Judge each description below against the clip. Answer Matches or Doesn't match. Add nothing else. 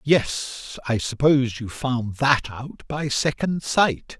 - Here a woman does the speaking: Doesn't match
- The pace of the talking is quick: Doesn't match